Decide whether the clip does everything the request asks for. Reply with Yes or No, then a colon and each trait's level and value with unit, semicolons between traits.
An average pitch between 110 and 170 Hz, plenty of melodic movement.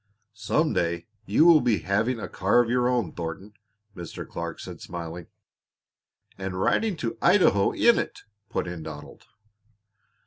No: low, 100 Hz; wide, 6.2 semitones